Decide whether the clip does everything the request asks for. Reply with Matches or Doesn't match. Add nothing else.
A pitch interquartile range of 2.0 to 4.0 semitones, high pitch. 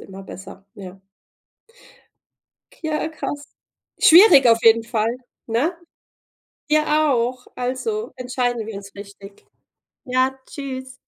Doesn't match